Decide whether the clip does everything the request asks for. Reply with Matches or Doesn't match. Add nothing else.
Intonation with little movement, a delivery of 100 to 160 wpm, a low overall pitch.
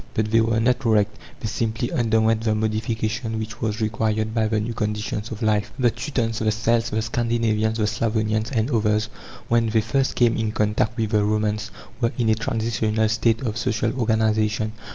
Doesn't match